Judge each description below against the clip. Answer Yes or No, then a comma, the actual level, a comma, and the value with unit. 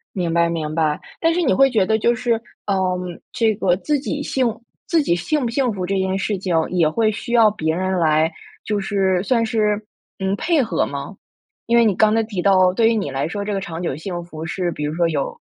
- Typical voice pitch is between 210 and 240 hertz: No, high, 195 Hz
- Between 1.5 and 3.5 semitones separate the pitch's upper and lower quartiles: No, average, 4.8 semitones